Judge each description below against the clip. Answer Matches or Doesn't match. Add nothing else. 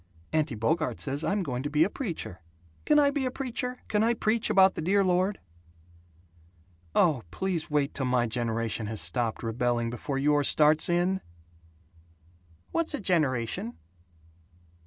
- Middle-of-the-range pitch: Matches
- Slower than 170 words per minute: Matches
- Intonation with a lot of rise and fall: Matches